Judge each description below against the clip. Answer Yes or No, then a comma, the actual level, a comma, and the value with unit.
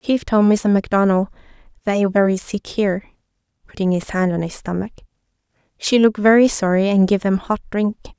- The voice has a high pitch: Yes, high, 200 Hz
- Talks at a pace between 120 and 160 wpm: Yes, average, 155 wpm